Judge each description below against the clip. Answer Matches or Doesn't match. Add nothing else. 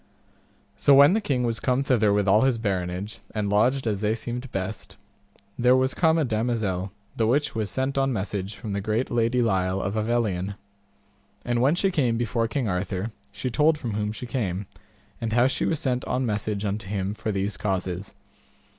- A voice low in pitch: Matches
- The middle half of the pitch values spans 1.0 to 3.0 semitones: Doesn't match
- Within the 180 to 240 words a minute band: Matches